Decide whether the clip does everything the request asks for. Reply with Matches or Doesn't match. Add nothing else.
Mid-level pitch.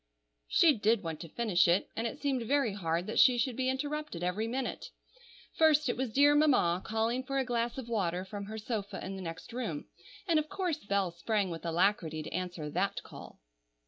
Doesn't match